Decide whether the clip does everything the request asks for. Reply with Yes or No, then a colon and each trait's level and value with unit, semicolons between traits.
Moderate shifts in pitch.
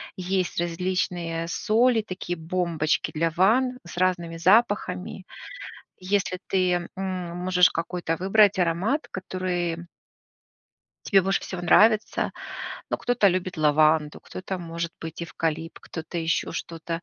No: narrow, 2.2 semitones